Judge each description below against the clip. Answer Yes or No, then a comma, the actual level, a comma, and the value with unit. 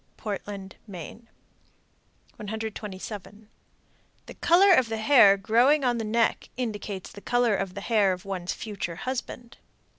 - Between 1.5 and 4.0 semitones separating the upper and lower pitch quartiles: Yes, average, 3.2 semitones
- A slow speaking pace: Yes, slow, 130 wpm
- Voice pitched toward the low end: No, high, 215 Hz